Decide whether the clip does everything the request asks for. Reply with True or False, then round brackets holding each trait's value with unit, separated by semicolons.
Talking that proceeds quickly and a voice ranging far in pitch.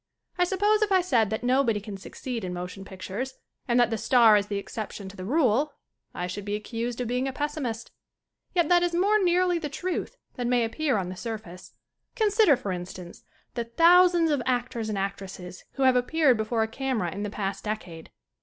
True (210 wpm; 6.8 semitones)